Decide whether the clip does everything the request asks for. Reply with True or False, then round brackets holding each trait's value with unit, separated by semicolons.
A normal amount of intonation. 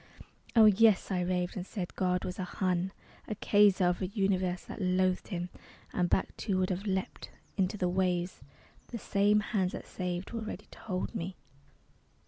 False (1.9 semitones)